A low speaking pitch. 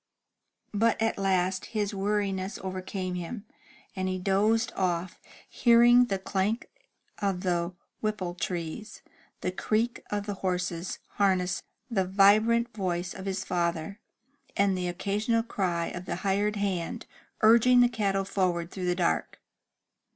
No: high, 195 Hz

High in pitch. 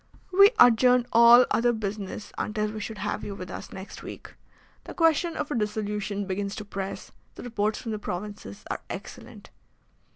Yes: high, 210 Hz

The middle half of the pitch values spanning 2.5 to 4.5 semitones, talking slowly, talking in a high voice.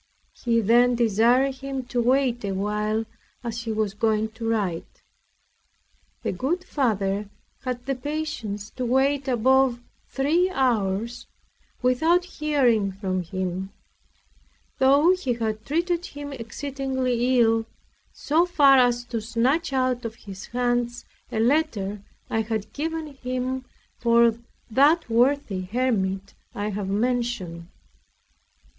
Yes: average, 3.9 semitones; slow, 120 wpm; high, 240 Hz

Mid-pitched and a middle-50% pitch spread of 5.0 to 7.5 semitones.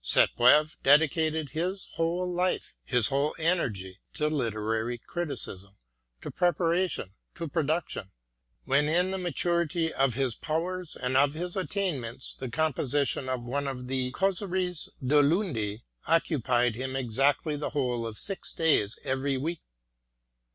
Yes: medium, 145 Hz; average, 5.3 semitones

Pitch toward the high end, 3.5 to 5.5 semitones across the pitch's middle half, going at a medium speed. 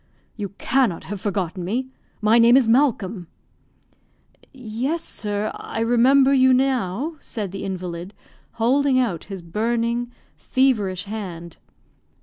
No: high, 225 Hz; average, 5.0 semitones; slow, 120 wpm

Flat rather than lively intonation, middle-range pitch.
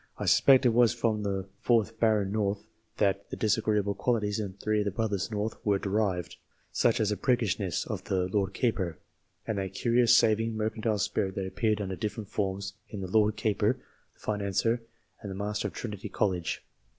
No: narrow, 2.2 semitones; low, 105 Hz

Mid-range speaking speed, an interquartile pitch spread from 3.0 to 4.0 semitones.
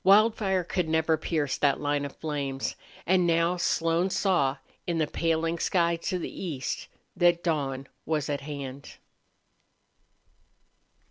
No: slow, 130 wpm; average, 3.3 semitones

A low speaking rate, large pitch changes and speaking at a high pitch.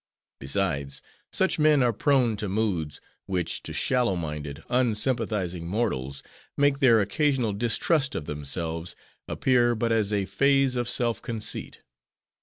No: slow, 130 wpm; wide, 6.2 semitones; low, 110 Hz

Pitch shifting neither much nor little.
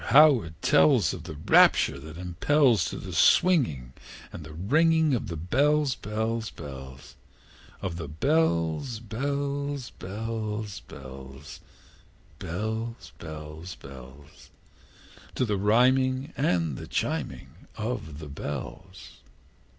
No: wide, 8.9 semitones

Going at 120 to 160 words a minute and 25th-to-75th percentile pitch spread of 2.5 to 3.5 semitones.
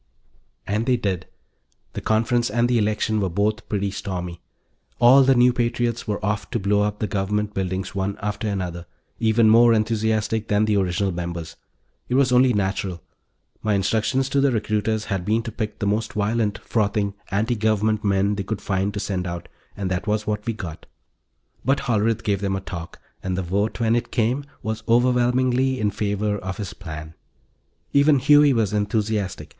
No: average, 180 wpm; average, 2.8 semitones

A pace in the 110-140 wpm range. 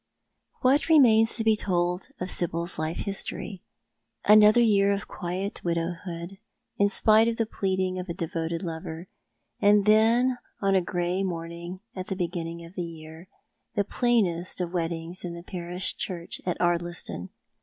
No: average, 155 wpm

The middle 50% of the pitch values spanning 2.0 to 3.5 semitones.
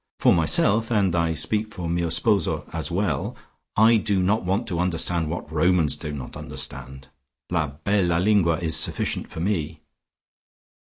No: average, 4.1 semitones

